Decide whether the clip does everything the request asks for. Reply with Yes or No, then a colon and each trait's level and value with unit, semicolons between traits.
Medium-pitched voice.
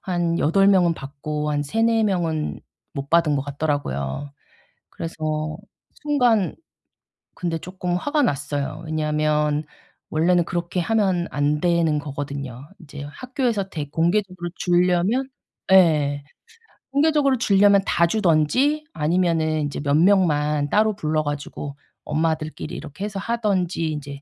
Yes: medium, 165 Hz